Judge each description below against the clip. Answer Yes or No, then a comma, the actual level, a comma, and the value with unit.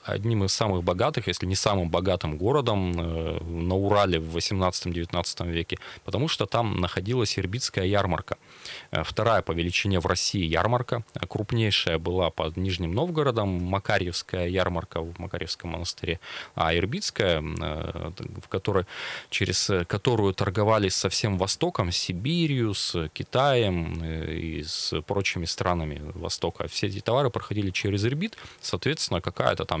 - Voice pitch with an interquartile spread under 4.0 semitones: No, average, 4.4 semitones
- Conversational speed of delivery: Yes, average, 125 wpm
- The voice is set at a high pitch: No, very low, 95 Hz